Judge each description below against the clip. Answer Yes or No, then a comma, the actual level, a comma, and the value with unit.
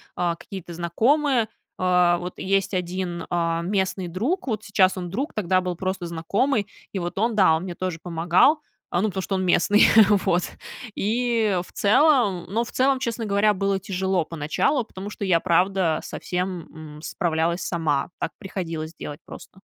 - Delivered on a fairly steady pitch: No, average, 3.2 semitones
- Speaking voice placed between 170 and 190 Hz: Yes, medium, 185 Hz